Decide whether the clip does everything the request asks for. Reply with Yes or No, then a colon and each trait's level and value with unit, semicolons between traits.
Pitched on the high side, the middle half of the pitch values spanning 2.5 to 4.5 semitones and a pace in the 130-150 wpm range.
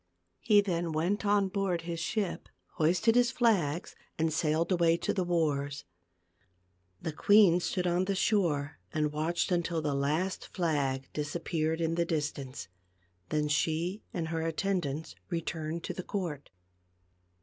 No: medium, 165 Hz; average, 3.1 semitones; average, 140 wpm